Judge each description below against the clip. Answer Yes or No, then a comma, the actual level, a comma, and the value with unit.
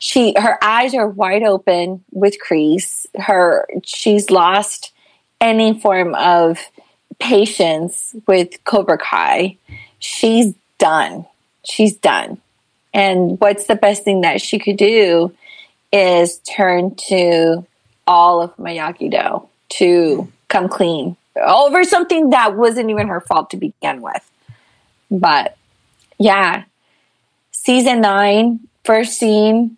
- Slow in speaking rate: Yes, slow, 115 wpm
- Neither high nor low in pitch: No, high, 205 Hz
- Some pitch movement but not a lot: Yes, average, 3.8 semitones